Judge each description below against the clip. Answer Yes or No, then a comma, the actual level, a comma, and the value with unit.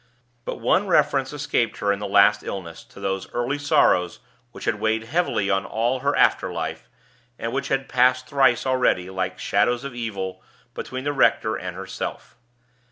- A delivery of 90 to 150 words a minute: No, average, 170 wpm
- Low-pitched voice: Yes, low, 120 Hz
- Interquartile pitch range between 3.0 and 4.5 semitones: No, average, 5.1 semitones